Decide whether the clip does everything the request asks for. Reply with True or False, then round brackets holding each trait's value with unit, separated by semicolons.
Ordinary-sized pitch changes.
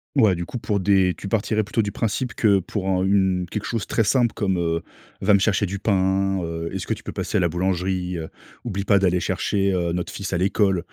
False (2.0 semitones)